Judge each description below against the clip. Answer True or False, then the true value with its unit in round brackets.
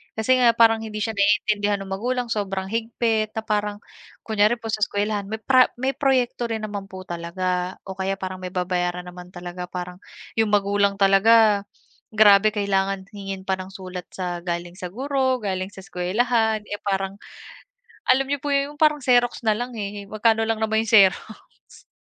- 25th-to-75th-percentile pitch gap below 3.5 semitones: True (3.0 semitones)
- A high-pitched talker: True (205 Hz)